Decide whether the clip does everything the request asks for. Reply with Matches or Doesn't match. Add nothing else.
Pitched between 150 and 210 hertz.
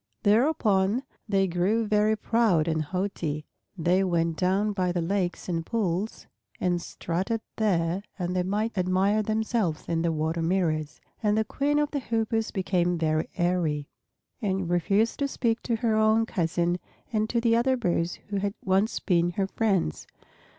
Matches